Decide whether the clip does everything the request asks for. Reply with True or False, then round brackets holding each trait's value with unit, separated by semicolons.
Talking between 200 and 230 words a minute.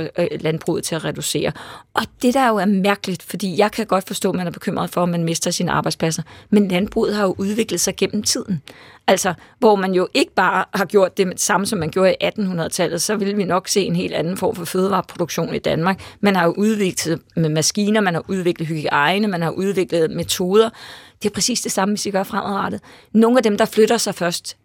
True (220 wpm)